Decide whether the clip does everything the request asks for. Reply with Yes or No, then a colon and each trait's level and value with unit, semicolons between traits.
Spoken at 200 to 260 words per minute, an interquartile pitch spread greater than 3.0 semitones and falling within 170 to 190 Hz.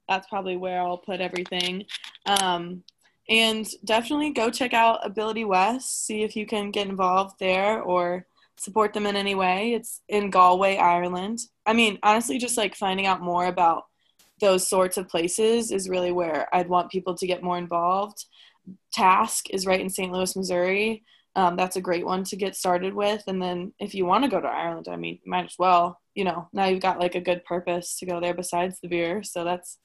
No: fast, 205 wpm; narrow, 2.5 semitones; medium, 185 Hz